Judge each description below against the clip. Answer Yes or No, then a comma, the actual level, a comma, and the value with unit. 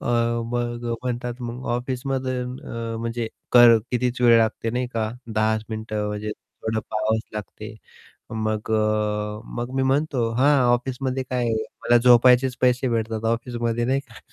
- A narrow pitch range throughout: Yes, narrow, 2.3 semitones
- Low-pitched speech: Yes, low, 120 Hz